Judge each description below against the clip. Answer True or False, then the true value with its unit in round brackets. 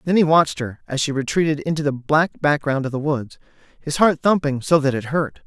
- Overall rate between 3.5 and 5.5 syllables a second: False (5.7 syllables/s)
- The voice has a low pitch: False (150 Hz)